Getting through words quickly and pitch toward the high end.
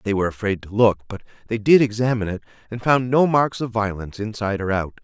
No: fast, 225 wpm; low, 110 Hz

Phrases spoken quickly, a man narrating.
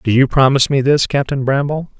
Yes: fast, 210 wpm; male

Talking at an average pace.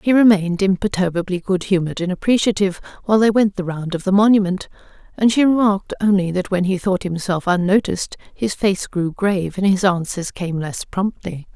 Yes: average, 180 wpm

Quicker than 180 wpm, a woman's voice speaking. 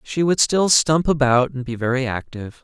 No: fast, 205 wpm; male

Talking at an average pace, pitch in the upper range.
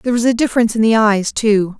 No: fast, 270 wpm; high, 220 Hz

